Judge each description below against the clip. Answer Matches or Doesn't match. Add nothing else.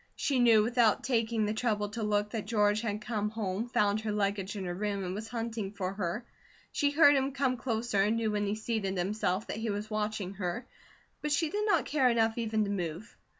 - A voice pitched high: Matches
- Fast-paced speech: Matches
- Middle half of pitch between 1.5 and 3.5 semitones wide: Matches